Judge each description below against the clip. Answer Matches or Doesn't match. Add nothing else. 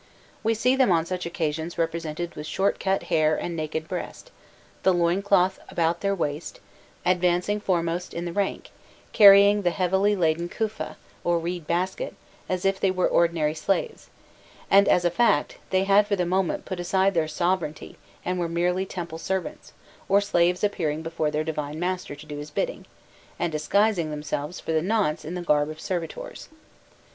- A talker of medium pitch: Matches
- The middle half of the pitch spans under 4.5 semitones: Matches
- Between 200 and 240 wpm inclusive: Doesn't match